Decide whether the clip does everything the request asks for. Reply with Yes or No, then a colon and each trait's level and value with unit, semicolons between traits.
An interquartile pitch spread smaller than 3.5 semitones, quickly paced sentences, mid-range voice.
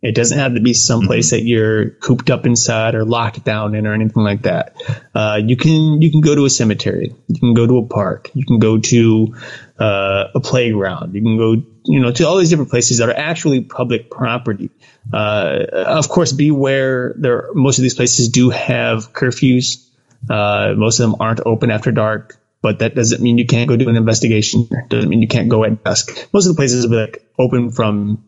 No: narrow, 2.6 semitones; fast, 220 wpm; low, 120 Hz